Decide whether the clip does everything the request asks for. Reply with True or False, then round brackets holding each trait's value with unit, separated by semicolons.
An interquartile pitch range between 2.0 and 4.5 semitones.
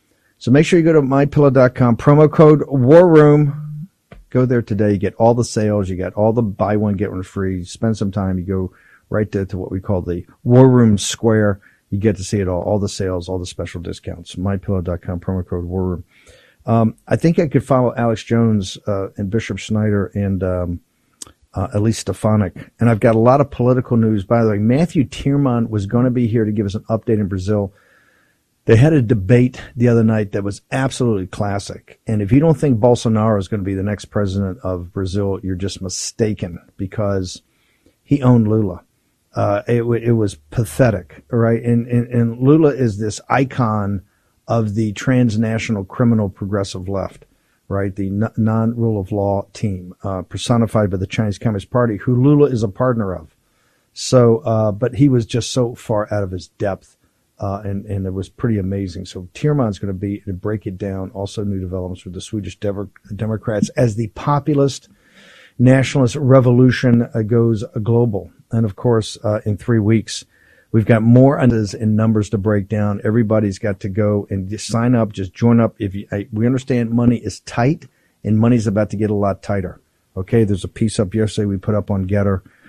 True (3.4 semitones)